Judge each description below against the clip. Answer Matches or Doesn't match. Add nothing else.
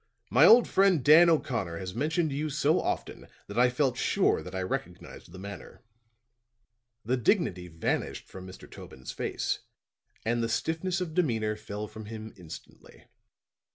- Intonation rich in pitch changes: Matches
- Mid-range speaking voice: Doesn't match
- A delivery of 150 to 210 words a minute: Matches